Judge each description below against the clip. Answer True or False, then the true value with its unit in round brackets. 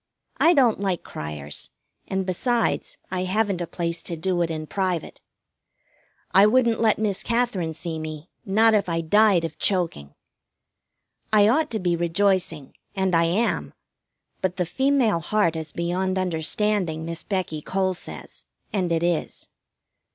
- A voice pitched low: False (185 Hz)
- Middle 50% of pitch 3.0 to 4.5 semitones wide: True (4.0 semitones)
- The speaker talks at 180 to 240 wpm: False (150 wpm)